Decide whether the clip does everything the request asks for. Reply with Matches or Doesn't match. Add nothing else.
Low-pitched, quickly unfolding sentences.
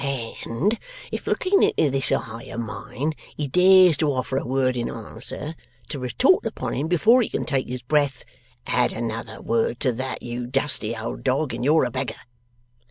Doesn't match